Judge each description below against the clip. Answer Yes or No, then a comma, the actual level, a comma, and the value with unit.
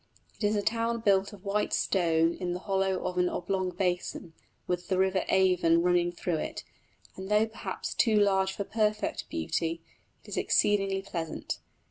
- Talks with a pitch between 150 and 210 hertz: Yes, high, 190 Hz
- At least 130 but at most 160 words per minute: No, average, 170 wpm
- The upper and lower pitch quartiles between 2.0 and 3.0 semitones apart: Yes, narrow, 2.5 semitones